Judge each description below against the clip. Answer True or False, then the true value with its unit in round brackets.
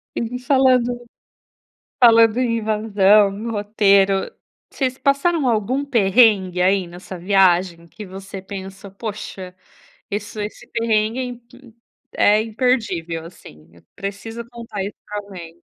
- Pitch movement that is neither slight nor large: True (3.5 semitones)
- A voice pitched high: True (210 Hz)